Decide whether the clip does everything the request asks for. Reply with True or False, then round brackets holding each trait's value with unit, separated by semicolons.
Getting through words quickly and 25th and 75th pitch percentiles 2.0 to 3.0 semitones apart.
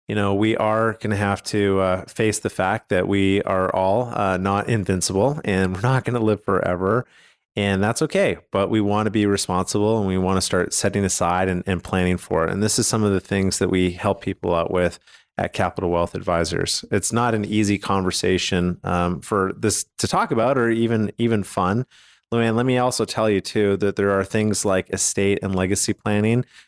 True (215 wpm; 2.7 semitones)